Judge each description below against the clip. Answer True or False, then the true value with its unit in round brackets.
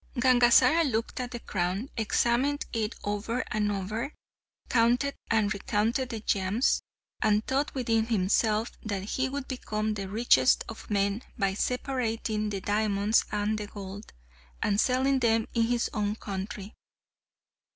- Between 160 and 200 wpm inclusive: False (135 wpm)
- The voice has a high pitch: True (220 Hz)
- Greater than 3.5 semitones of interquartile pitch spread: False (2.9 semitones)